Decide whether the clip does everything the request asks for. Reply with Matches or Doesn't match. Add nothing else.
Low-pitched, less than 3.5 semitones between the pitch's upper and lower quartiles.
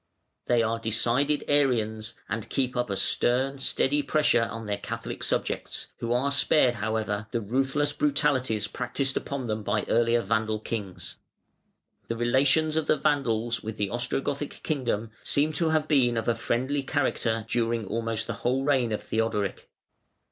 Doesn't match